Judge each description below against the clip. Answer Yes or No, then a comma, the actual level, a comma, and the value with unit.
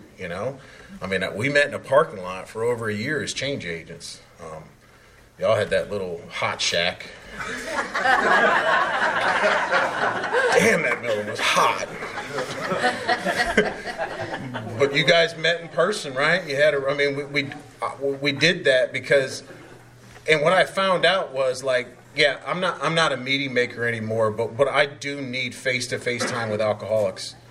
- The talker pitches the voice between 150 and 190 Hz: No, low, 135 Hz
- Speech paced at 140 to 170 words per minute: Yes, average, 160 wpm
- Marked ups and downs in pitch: No, average, 3.5 semitones